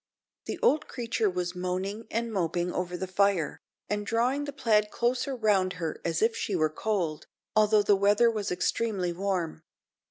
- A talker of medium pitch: No, high, 200 Hz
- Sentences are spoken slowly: No, average, 165 wpm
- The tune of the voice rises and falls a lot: No, average, 4.0 semitones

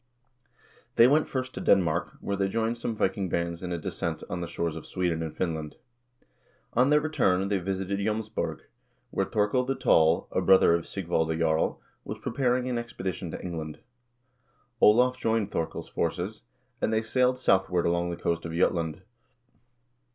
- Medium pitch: No, very low, 95 Hz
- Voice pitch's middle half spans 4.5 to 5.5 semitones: Yes, average, 4.9 semitones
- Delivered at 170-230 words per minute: Yes, average, 175 wpm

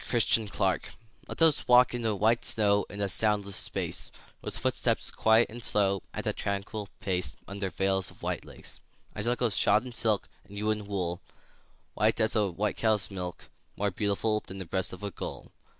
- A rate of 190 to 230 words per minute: Yes, average, 195 wpm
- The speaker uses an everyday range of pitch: No, narrow, 2.2 semitones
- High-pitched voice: No, low, 105 Hz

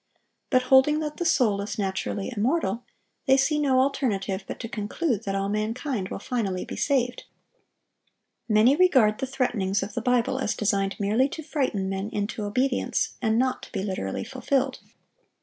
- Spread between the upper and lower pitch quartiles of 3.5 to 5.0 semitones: Yes, average, 4.7 semitones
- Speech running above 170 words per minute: No, average, 165 wpm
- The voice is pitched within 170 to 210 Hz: No, high, 230 Hz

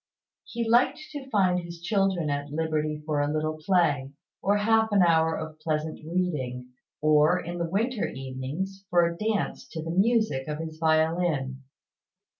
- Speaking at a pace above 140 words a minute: Yes, average, 160 wpm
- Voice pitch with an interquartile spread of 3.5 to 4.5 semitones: Yes, average, 4.1 semitones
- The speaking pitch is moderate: Yes, medium, 165 Hz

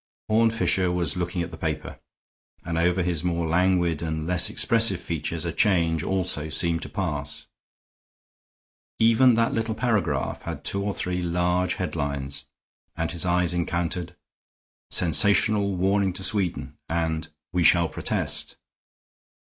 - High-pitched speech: No, very low, 90 Hz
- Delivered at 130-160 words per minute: Yes, slow, 135 wpm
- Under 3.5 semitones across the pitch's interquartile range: Yes, average, 2.7 semitones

